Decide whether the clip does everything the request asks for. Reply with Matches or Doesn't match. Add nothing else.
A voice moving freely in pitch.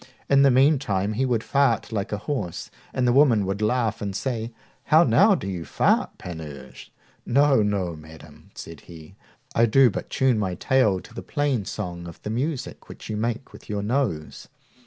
Matches